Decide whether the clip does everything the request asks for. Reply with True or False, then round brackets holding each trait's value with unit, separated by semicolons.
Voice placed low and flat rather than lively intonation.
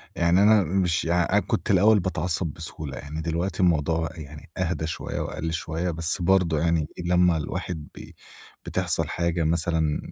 True (85 Hz; 2.1 semitones)